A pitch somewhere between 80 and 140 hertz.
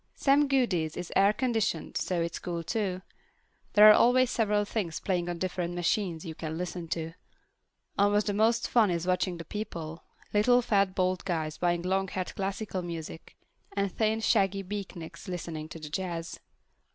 No: medium, 185 Hz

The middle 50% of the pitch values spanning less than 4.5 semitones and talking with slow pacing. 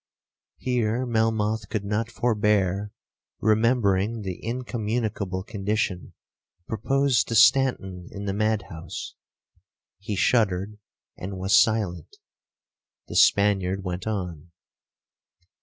Yes: average, 2.8 semitones; slow, 90 wpm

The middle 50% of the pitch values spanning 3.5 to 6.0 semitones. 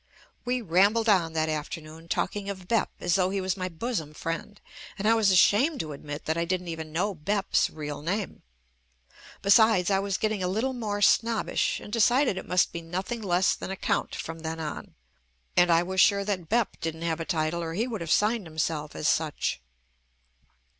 Yes: average, 4.2 semitones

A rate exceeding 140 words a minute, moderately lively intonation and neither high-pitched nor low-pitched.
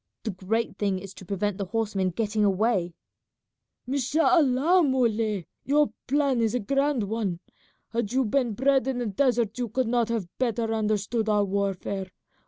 No: average, 160 wpm; average, 4.1 semitones; high, 225 Hz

